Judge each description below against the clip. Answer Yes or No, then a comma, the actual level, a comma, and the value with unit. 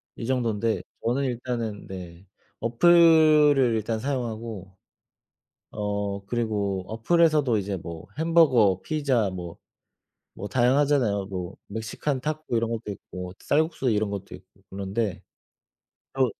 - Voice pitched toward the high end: No, low, 115 Hz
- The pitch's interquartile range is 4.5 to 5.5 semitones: Yes, average, 5.2 semitones